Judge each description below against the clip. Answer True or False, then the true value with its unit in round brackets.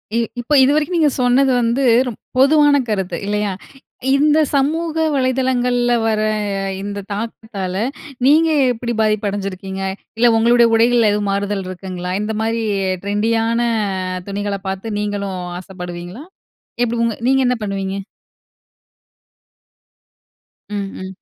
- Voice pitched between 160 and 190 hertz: False (225 Hz)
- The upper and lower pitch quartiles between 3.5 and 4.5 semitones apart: True (4.0 semitones)